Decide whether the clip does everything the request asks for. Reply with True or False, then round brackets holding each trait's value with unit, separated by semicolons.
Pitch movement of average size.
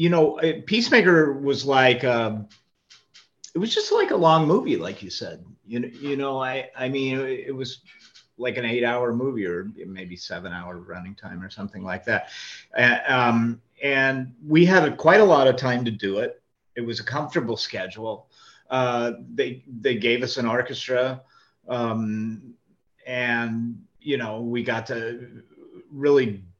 True (3.2 semitones)